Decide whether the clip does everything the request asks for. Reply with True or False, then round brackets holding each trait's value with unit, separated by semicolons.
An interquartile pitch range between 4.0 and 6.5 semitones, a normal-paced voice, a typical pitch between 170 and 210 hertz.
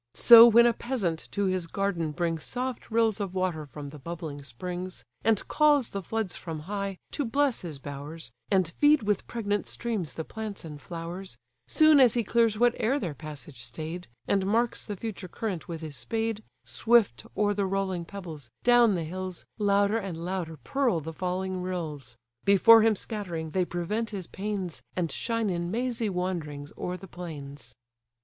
True (5.2 semitones; 170 wpm; 185 Hz)